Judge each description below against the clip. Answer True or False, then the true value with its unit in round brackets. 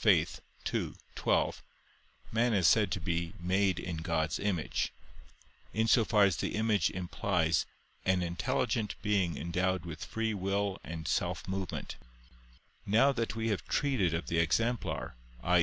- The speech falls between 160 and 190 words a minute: False (140 wpm)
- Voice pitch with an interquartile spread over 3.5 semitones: True (4.2 semitones)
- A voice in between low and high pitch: False (95 Hz)